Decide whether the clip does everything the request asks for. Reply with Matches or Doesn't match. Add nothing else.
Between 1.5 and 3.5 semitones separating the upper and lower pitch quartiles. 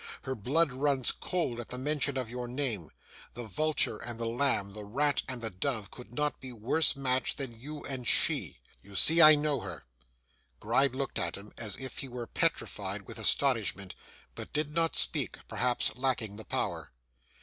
Doesn't match